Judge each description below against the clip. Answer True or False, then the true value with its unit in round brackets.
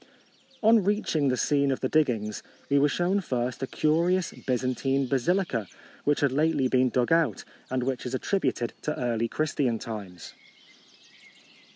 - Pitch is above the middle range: False (135 Hz)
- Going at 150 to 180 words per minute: True (160 wpm)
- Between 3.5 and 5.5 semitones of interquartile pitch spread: True (4.2 semitones)